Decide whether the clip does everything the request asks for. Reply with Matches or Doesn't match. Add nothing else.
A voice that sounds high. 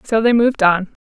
Matches